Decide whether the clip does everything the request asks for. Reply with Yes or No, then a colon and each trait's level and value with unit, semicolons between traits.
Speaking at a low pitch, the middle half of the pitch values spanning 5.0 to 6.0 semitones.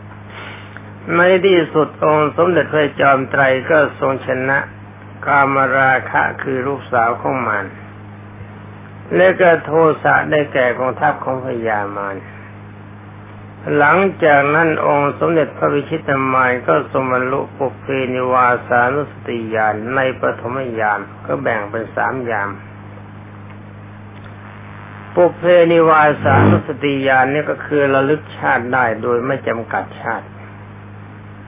Yes: low, 120 Hz; average, 5.3 semitones